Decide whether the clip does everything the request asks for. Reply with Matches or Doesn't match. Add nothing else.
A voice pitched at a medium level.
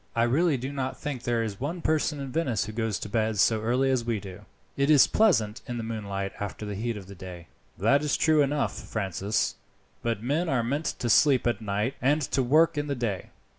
Doesn't match